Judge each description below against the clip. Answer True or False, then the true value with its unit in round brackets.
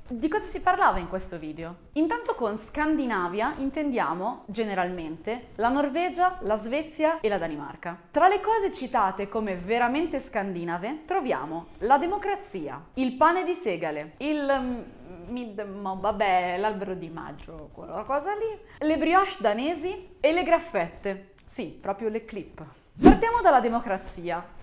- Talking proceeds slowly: False (135 wpm)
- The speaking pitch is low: False (240 Hz)